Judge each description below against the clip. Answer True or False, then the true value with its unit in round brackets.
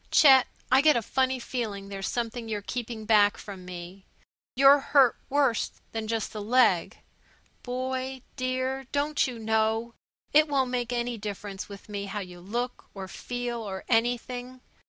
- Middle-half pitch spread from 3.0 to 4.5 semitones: True (3.8 semitones)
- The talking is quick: False (155 wpm)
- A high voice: True (235 Hz)